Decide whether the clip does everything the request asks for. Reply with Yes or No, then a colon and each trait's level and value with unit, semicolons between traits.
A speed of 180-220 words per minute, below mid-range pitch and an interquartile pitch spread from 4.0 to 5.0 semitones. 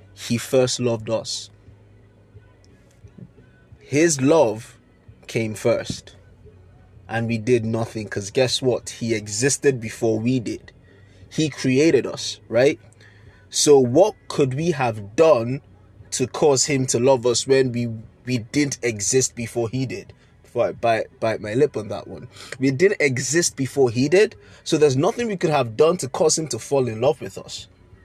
No: average, 160 wpm; low, 120 Hz; average, 4.4 semitones